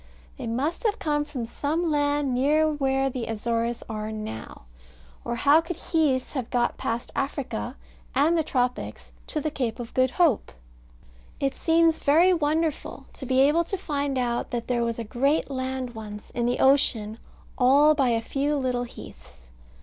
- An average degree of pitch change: Yes, average, 3.9 semitones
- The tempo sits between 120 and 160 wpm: No, average, 170 wpm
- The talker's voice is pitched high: Yes, very high, 265 Hz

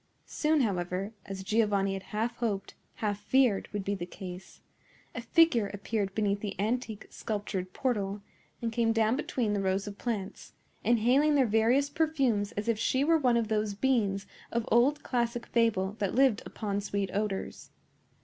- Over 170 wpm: No, average, 160 wpm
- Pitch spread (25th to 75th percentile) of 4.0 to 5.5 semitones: No, average, 3.2 semitones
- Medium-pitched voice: No, high, 215 Hz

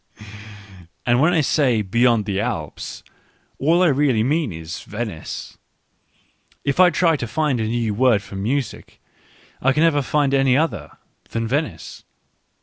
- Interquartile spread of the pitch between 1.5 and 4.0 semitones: No, average, 5.3 semitones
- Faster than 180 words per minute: No, average, 145 wpm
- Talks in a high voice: No, low, 125 Hz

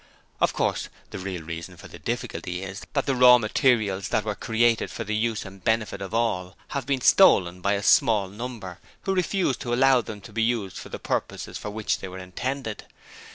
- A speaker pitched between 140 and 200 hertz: No, low, 110 Hz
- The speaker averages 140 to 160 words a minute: No, fast, 205 wpm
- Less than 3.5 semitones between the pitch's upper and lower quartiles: No, average, 4.3 semitones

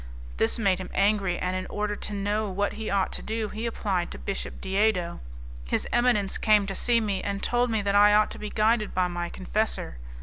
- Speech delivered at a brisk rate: Yes, fast, 215 wpm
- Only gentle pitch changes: Yes, narrow, 2.2 semitones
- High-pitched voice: Yes, high, 205 Hz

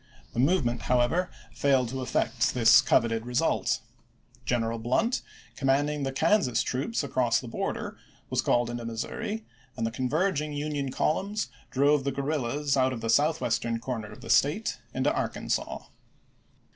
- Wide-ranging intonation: No, average, 3.8 semitones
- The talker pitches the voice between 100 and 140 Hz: Yes, low, 135 Hz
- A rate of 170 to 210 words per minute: No, average, 155 wpm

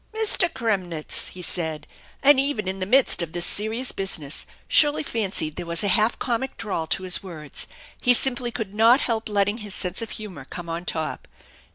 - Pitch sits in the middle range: No, high, 205 Hz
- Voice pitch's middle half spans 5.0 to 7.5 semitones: Yes, average, 5.3 semitones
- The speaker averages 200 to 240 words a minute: No, average, 190 wpm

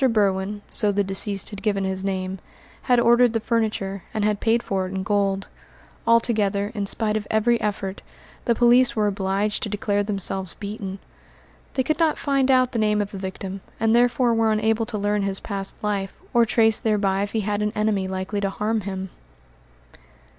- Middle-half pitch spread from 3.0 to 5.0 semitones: No, narrow, 2.5 semitones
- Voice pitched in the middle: No, high, 210 Hz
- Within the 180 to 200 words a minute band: Yes, average, 190 wpm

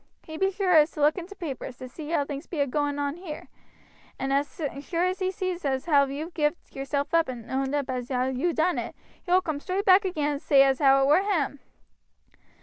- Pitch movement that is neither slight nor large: Yes, average, 4.4 semitones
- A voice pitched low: No, very high, 295 Hz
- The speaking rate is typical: No, fast, 240 wpm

